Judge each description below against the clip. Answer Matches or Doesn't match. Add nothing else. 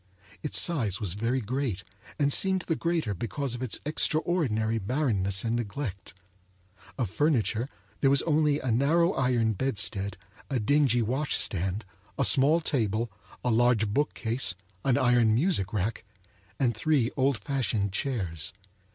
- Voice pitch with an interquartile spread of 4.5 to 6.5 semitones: Matches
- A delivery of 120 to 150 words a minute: Matches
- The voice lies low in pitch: Matches